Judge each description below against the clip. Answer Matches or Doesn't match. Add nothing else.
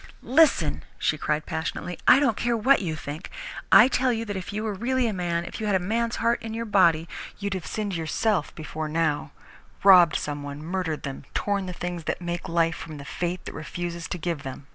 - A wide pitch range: Doesn't match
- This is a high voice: Doesn't match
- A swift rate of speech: Matches